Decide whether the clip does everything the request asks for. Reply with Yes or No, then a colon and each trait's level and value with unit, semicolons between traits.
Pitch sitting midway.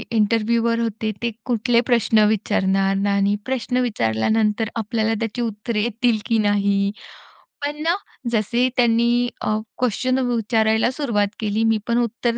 No: high, 225 Hz